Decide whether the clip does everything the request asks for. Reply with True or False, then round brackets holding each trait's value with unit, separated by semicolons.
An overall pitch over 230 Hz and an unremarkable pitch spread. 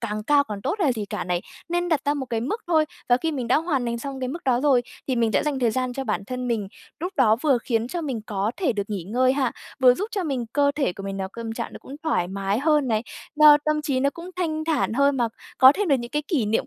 True (260 Hz; 4.8 semitones)